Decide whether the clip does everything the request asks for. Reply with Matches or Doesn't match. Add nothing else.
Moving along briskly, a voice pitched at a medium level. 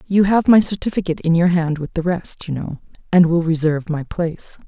Matches